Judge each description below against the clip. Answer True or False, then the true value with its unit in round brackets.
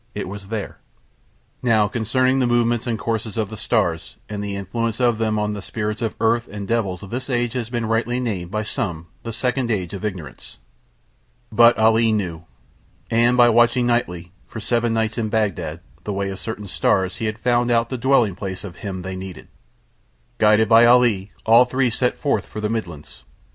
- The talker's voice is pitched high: False (110 Hz)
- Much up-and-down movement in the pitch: False (3.0 semitones)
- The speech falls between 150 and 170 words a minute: False (190 wpm)